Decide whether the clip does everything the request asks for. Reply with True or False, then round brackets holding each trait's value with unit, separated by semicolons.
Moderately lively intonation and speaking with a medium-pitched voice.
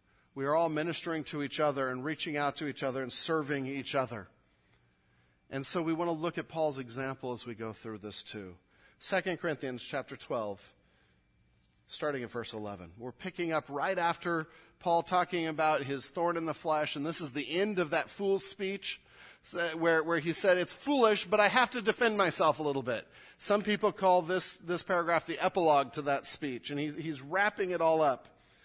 True (4.6 semitones; 155 Hz)